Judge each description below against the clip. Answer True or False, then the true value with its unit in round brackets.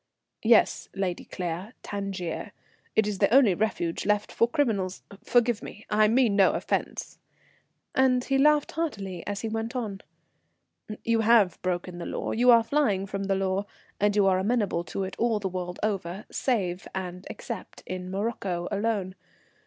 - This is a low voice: False (205 Hz)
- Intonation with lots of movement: False (3.5 semitones)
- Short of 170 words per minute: True (160 wpm)